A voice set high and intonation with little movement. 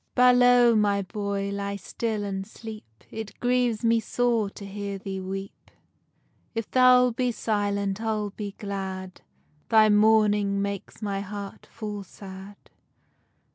Yes: high, 205 Hz; narrow, 2.1 semitones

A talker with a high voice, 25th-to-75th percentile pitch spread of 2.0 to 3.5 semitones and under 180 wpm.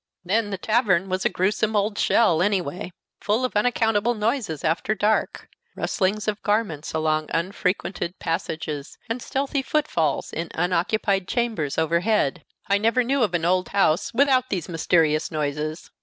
No: high, 195 Hz; average, 5.2 semitones; average, 150 wpm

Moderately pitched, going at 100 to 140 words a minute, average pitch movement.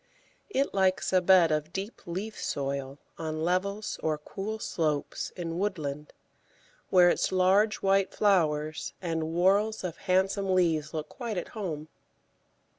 Yes: medium, 180 Hz; slow, 135 wpm; average, 3.8 semitones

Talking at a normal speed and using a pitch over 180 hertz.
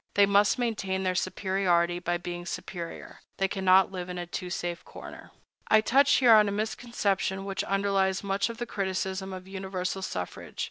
Yes: average, 170 wpm; high, 190 Hz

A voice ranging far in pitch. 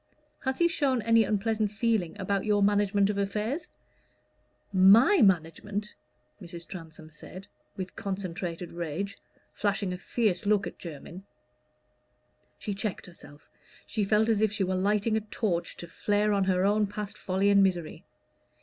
No: narrow, 2.5 semitones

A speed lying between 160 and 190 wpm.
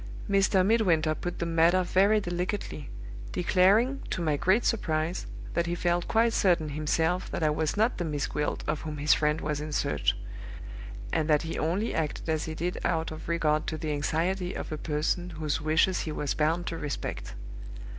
Yes: average, 185 wpm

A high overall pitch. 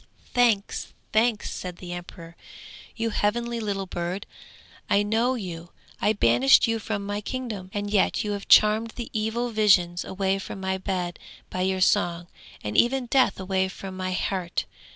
Yes: high, 200 Hz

